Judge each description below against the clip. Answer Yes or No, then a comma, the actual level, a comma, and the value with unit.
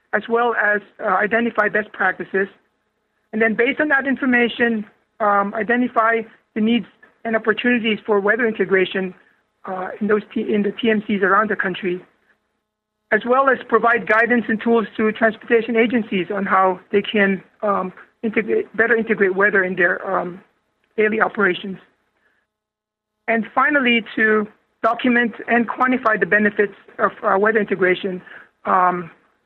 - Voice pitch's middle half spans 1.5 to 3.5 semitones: Yes, narrow, 2.6 semitones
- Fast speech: No, average, 140 wpm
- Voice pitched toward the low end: No, high, 215 Hz